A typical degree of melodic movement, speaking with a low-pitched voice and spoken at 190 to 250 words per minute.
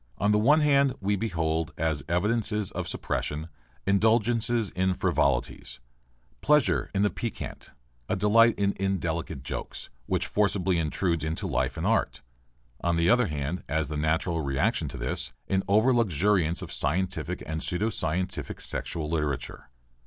No: average, 4.9 semitones; very low, 95 Hz; average, 145 wpm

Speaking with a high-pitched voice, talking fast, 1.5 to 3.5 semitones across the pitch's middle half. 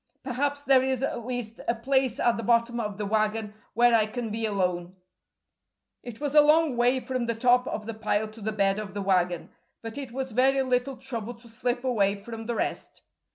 Yes: high, 235 Hz; fast, 210 wpm; average, 3.1 semitones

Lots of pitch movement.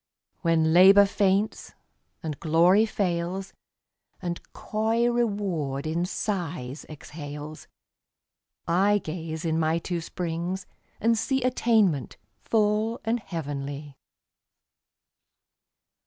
No: average, 4.7 semitones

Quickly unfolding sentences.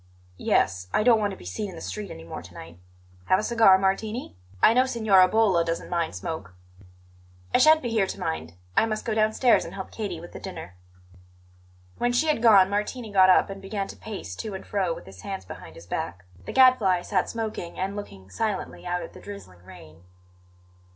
Yes: fast, 210 wpm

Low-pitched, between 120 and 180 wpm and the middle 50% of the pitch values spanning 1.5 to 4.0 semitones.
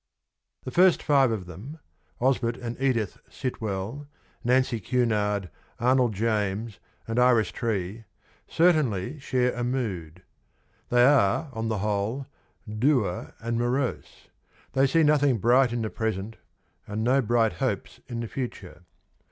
Yes: low, 115 Hz; slow, 135 wpm; average, 3.6 semitones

